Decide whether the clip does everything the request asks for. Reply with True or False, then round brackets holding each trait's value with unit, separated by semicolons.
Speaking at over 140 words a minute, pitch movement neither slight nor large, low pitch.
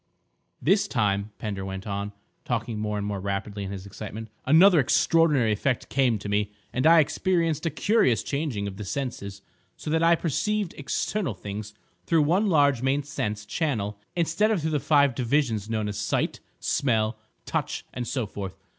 False (175 wpm; 7.0 semitones; 120 Hz)